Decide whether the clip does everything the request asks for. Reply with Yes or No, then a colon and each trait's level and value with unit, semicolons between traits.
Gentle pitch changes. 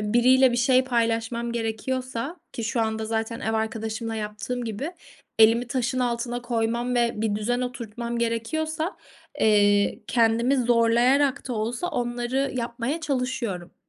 Yes: narrow, 2.0 semitones